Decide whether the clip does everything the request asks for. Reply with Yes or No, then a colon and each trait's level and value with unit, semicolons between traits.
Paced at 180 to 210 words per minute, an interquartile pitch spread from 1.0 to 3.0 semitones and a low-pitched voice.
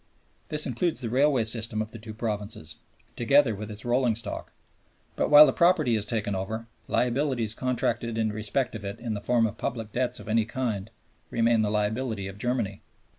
Yes: average, 185 wpm; narrow, 2.6 semitones; low, 115 Hz